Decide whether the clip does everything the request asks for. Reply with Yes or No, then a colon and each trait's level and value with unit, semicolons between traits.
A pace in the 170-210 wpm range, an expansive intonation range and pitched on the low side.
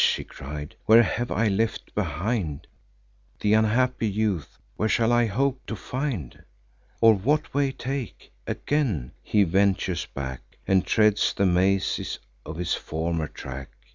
No: average, 140 wpm; wide, 5.8 semitones; low, 105 Hz